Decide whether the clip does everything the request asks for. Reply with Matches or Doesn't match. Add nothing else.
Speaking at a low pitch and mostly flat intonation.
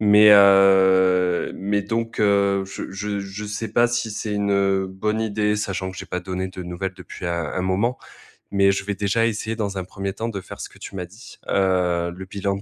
Matches